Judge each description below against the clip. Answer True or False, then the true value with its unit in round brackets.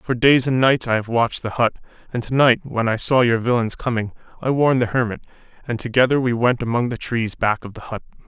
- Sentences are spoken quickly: True (230 wpm)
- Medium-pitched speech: False (120 Hz)